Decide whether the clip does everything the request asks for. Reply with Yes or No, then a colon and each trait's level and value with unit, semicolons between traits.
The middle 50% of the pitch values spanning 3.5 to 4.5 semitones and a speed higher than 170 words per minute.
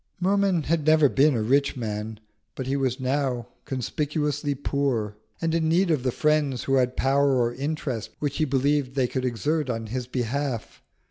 No: average, 3.0 semitones; average, 180 wpm